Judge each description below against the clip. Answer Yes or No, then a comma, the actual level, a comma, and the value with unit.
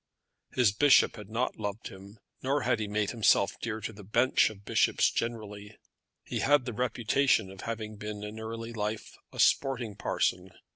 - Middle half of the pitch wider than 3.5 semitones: No, narrow, 2.4 semitones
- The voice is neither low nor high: No, low, 110 Hz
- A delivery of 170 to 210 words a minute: Yes, average, 175 wpm